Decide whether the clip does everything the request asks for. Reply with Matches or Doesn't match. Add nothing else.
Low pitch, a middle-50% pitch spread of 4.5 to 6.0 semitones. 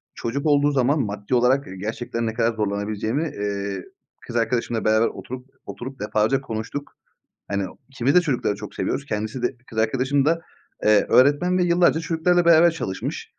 Matches